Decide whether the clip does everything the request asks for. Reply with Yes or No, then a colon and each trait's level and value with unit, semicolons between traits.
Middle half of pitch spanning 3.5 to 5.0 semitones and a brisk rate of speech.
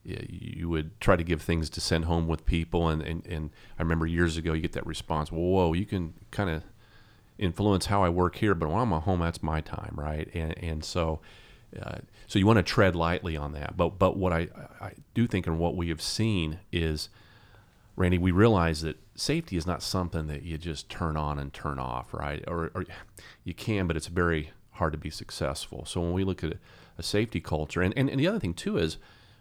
Yes: average, 3.9 semitones; fast, 225 wpm